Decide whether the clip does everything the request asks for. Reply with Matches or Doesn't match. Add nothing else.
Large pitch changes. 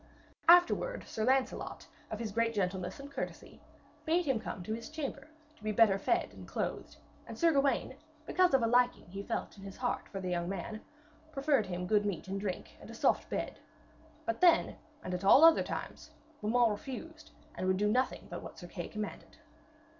Matches